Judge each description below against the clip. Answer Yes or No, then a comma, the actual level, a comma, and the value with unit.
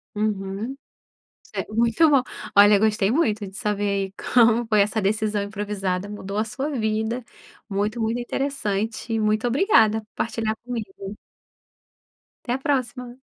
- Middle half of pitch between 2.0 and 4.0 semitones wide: Yes, narrow, 2.6 semitones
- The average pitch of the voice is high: Yes, high, 220 Hz